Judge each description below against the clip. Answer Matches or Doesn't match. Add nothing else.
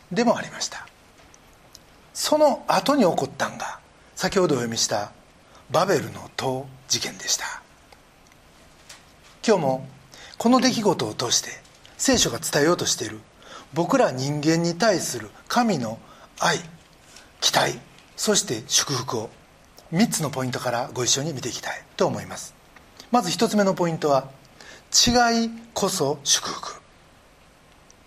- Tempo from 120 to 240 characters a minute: Matches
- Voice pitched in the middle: Matches